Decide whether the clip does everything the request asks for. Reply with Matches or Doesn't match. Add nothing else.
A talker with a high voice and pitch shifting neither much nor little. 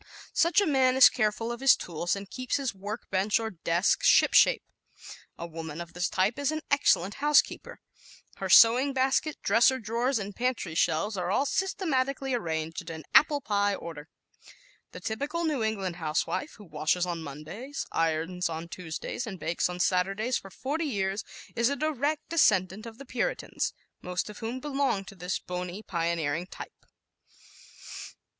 Doesn't match